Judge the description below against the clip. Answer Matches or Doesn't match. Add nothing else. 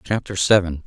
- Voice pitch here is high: Doesn't match